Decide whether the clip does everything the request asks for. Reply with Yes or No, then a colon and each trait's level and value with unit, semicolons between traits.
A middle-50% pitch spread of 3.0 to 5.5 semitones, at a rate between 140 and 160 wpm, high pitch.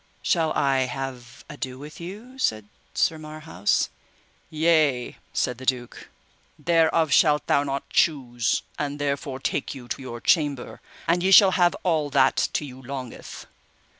No: average, 3.7 semitones; average, 145 wpm; medium, 140 Hz